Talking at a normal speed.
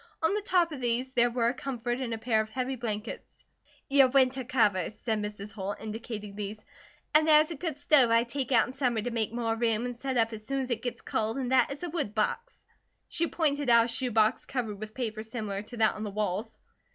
No: fast, 240 wpm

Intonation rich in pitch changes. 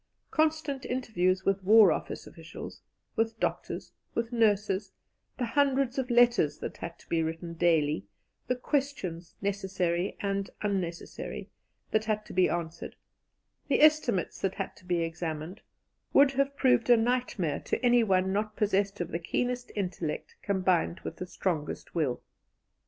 Yes: wide, 5.8 semitones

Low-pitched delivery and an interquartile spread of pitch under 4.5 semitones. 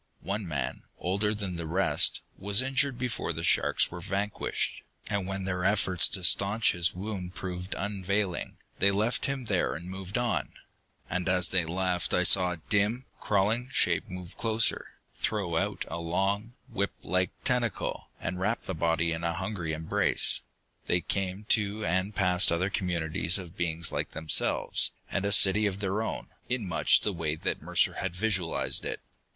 Yes: very low, 95 Hz; average, 2.8 semitones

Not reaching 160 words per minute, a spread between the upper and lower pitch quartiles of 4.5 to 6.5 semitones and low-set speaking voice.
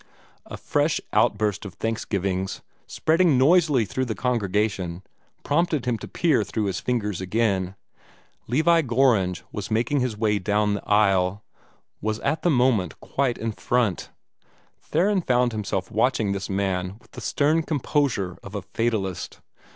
Yes: average, 145 wpm; average, 4.9 semitones; low, 110 Hz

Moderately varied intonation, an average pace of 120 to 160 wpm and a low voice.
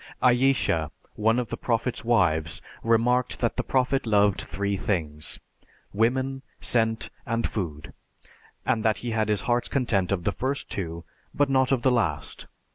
Yes: average, 4.1 semitones; average, 155 wpm; low, 115 Hz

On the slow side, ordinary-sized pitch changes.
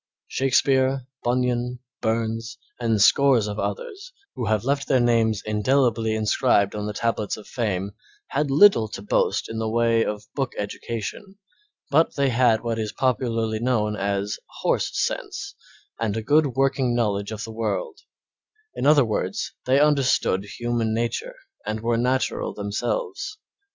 No: average, 150 wpm; average, 3.5 semitones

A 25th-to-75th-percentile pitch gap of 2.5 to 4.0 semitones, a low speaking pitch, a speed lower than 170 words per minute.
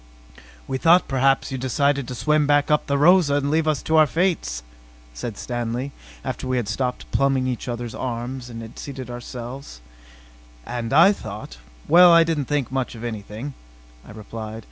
No: average, 3.7 semitones; low, 130 Hz; average, 180 wpm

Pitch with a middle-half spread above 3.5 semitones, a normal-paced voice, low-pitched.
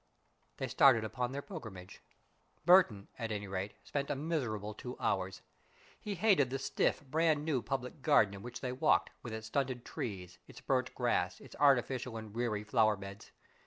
Yes: average, 4.9 semitones; average, 170 wpm; low, 120 Hz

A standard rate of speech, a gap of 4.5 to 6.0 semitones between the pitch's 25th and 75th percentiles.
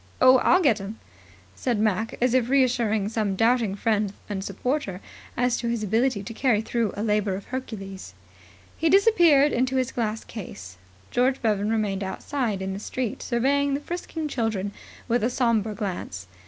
No: average, 170 wpm; average, 4.0 semitones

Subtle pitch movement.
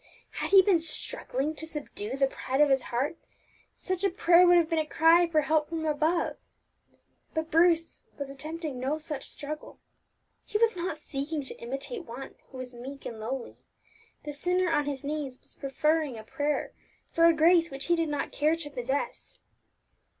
No: average, 3.4 semitones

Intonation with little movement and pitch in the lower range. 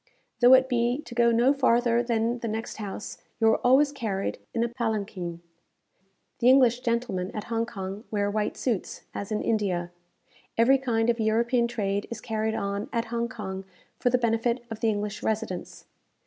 No: narrow, 2.3 semitones; high, 230 Hz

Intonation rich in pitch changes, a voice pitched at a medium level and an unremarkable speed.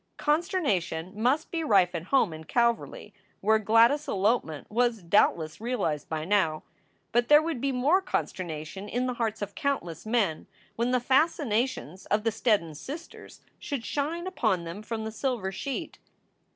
No: wide, 6.2 semitones; high, 225 Hz; average, 160 wpm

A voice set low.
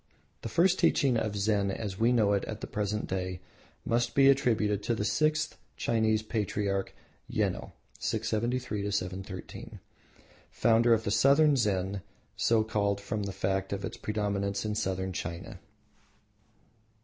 Yes: low, 105 Hz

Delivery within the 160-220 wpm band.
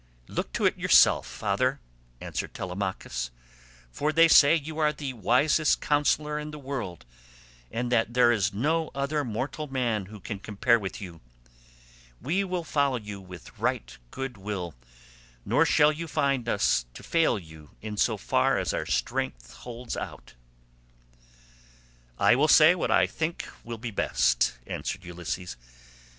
No: average, 150 wpm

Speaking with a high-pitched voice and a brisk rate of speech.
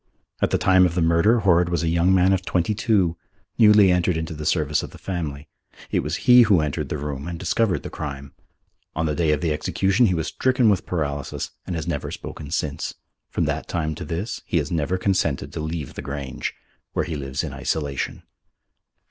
No: very low, 85 Hz; fast, 210 wpm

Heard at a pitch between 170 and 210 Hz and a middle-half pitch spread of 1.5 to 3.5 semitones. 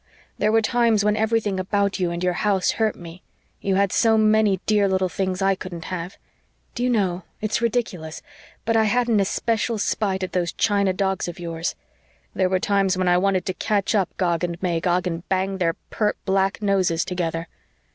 Yes: high, 190 Hz; average, 2.7 semitones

